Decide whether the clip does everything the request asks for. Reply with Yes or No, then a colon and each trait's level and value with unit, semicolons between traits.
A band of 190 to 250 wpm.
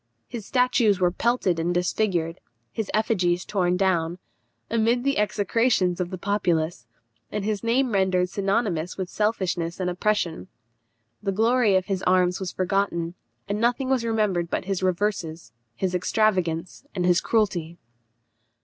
No: average, 140 wpm